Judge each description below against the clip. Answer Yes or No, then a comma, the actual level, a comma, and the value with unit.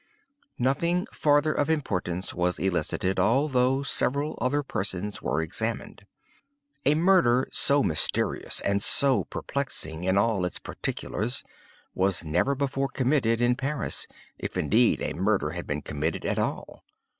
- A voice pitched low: Yes, low, 120 Hz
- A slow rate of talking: Yes, slow, 130 wpm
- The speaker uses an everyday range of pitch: No, wide, 7.2 semitones